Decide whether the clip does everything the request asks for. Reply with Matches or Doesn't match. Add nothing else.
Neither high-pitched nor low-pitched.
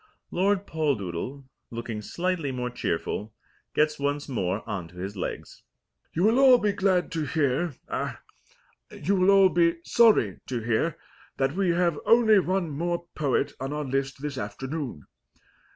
Matches